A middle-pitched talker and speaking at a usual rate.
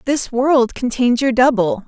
No: very high, 250 Hz; average, 160 wpm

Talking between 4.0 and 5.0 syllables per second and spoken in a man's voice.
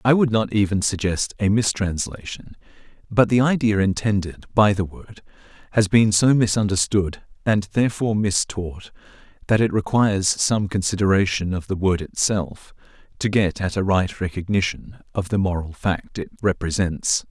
Yes: 4.8 syllables/s; male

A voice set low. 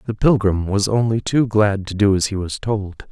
Yes: low, 105 Hz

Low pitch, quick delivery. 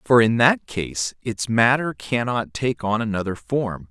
No: low, 110 Hz; average, 170 wpm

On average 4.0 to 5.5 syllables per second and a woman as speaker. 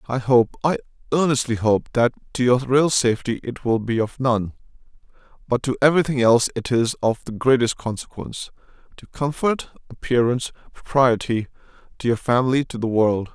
No: 5.4 syllables/s; male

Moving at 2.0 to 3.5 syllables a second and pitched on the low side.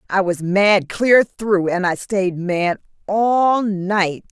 No: 2.9 syllables/s; high, 195 Hz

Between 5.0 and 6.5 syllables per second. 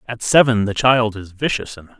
Yes: 6.0 syllables/s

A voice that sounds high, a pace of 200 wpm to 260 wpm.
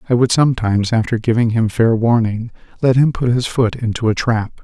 No: low, 115 Hz; fast, 205 wpm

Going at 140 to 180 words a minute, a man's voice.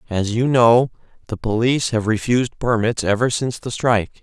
Yes: average, 170 wpm; male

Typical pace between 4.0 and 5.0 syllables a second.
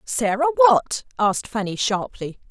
Yes: 4.4 syllables/s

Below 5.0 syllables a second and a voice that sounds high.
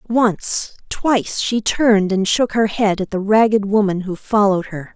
Yes: 4.6 syllables/s; high, 205 Hz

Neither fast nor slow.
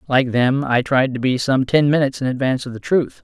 No: fast, 260 wpm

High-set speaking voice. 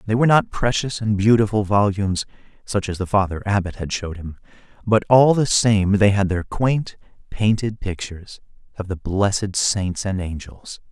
No: low, 100 Hz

